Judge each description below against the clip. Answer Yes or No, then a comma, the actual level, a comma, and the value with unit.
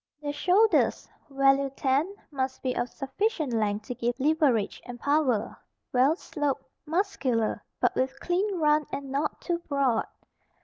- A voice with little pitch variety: No, average, 3.6 semitones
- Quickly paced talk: No, average, 140 wpm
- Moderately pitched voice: No, very high, 275 Hz